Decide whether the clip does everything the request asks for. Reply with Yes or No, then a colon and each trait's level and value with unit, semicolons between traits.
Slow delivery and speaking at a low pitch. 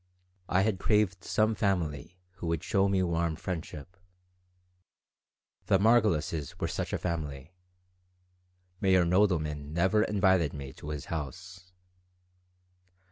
Yes: slow, 115 wpm; very low, 90 Hz